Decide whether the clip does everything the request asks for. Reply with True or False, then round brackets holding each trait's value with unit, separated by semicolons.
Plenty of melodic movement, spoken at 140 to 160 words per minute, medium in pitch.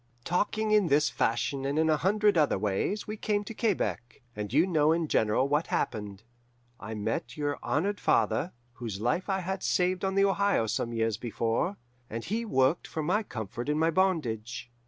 False (8.7 semitones; 185 wpm; 150 Hz)